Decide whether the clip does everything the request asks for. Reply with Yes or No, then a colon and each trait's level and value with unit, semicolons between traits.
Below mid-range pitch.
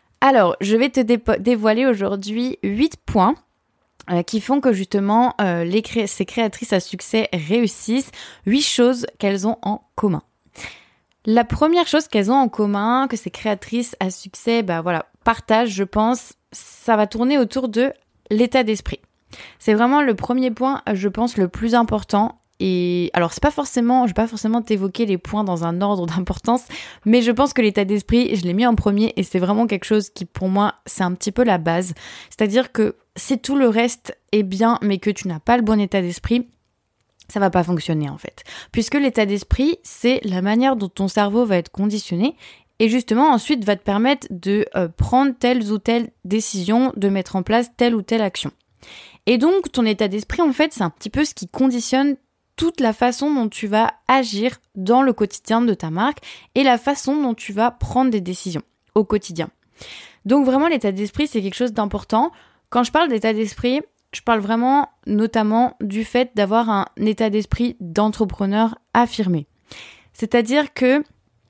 No: high, 225 Hz